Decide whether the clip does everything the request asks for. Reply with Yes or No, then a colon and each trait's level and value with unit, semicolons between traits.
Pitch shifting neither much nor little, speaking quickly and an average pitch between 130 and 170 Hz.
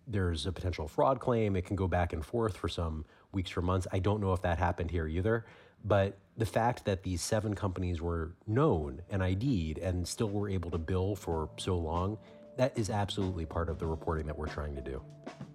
No: average, 3.4 semitones; fast, 215 wpm; very low, 95 Hz